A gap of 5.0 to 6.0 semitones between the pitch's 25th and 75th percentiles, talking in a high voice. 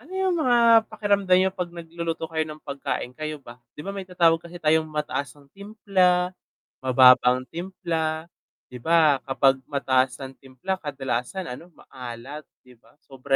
No: wide, 5.5 semitones; medium, 160 Hz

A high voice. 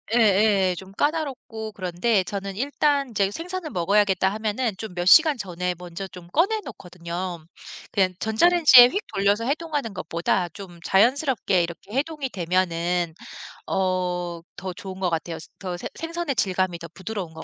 Yes: high, 195 Hz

